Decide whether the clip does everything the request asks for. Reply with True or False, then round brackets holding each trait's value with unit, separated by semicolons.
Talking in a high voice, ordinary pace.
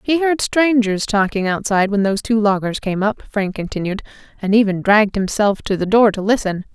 True (210 Hz; 195 wpm)